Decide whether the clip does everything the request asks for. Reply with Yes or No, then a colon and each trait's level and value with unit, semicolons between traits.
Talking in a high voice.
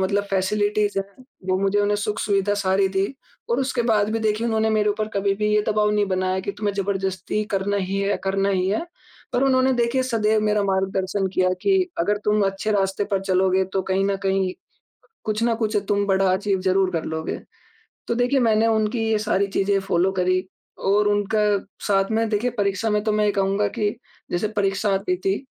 Yes: high, 205 Hz